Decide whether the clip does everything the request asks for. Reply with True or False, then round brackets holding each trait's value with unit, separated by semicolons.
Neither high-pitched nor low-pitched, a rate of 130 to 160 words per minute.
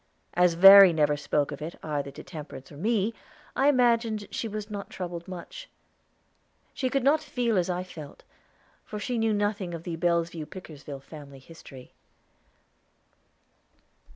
True (180 Hz; 150 wpm)